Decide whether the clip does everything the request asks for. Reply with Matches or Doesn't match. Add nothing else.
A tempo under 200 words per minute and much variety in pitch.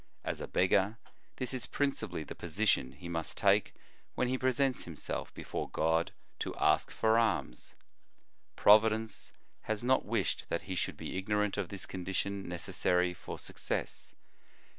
Doesn't match